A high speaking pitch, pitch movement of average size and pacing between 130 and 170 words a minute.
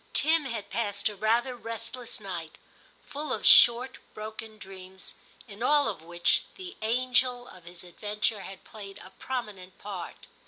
Yes: high, 215 Hz; average, 4.4 semitones; average, 150 wpm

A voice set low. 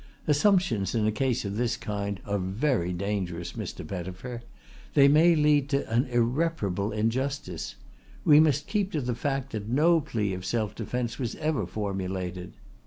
Yes: low, 115 Hz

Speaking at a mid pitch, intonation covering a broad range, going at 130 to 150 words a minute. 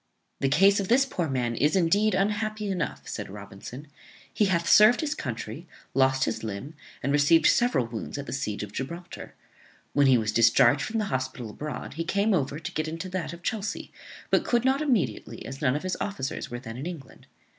No: medium, 155 Hz; wide, 7.2 semitones; average, 200 wpm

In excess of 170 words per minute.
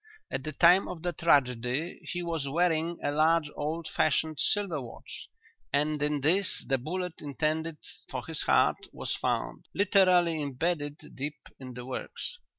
No: average, 155 wpm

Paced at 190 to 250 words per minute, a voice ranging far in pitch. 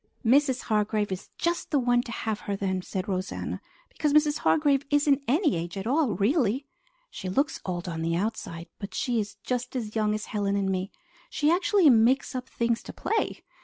Yes: average, 195 wpm; wide, 6.0 semitones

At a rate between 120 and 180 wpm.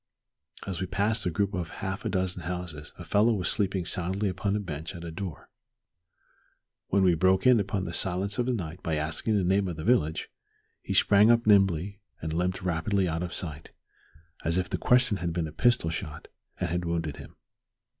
No: average, 200 wpm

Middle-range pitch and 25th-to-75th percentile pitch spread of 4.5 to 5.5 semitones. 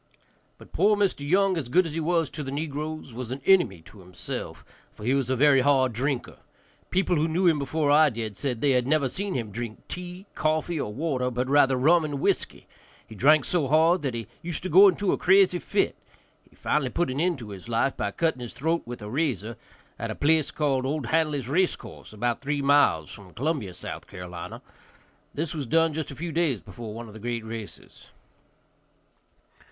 Yes: medium, 145 Hz; average, 5.1 semitones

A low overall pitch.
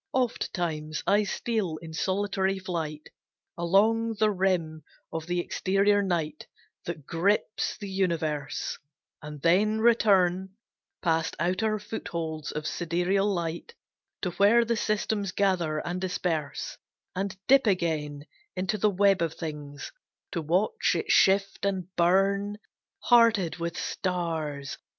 No: medium, 185 Hz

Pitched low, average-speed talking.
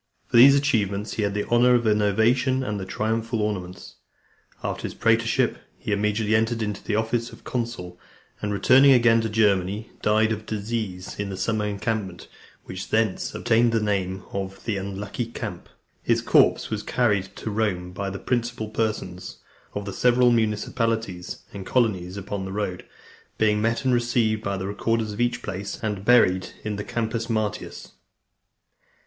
Yes: low, 110 Hz; average, 165 wpm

